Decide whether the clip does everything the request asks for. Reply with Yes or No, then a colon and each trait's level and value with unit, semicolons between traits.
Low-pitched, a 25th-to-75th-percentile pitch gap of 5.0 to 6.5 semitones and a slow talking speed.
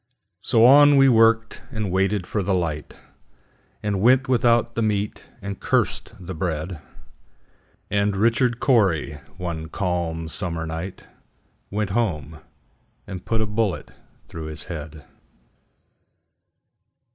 Yes: very low, 95 Hz; wide, 5.5 semitones; slow, 110 wpm